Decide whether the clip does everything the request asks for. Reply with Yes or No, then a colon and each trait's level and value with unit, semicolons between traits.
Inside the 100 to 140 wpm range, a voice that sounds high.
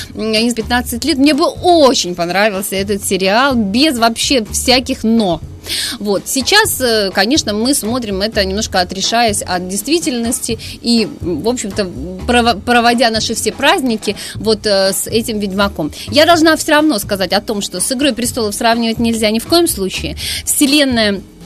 No: average, 150 wpm; high, 230 Hz